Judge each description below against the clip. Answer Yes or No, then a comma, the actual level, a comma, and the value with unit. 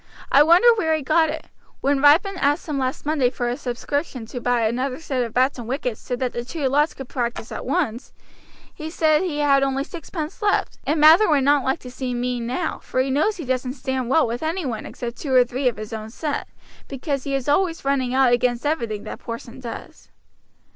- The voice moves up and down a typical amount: Yes, average, 3.7 semitones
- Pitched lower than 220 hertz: No, very high, 270 Hz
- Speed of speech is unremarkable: No, fast, 220 wpm